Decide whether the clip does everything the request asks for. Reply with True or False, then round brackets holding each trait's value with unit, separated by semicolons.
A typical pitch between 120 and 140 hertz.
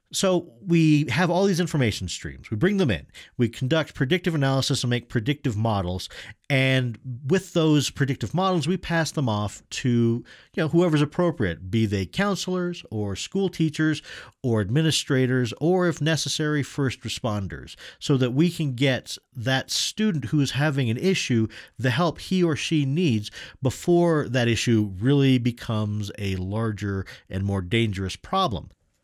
True (135 Hz)